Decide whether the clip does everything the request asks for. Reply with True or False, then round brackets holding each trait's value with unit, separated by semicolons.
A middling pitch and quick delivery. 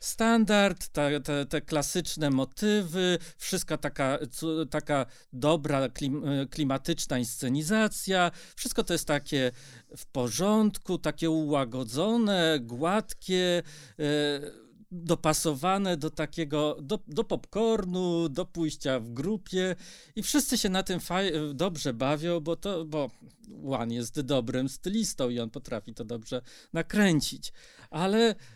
False (160 Hz; 110 wpm)